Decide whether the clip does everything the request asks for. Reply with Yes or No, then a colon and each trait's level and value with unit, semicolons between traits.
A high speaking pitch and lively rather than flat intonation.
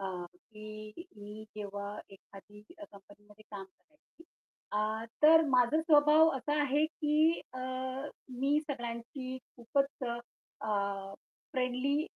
Yes: high, 240 Hz; wide, 6.0 semitones